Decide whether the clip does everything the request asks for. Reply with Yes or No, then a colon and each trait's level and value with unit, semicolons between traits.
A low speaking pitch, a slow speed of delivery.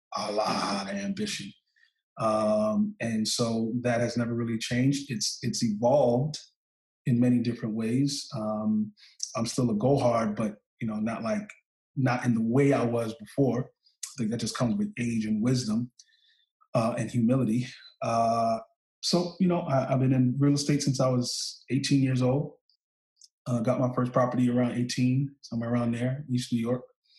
No: low, 125 Hz; average, 170 wpm